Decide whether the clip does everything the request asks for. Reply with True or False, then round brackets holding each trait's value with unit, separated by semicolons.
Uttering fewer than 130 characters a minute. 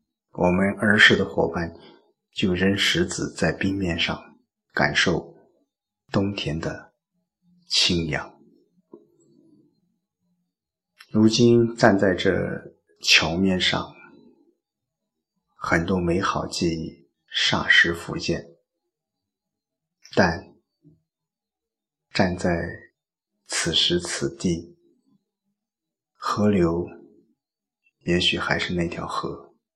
True (115 characters per minute)